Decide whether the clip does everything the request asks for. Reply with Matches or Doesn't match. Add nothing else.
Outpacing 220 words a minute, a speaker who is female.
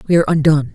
Doesn't match